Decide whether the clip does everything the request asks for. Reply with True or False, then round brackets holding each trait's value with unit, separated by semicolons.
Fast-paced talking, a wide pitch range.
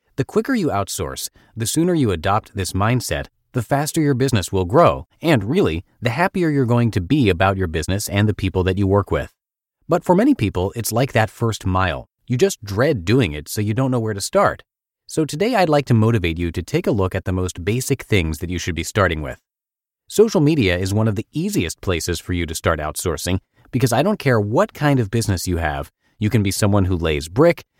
True (230 wpm; 6.2 semitones)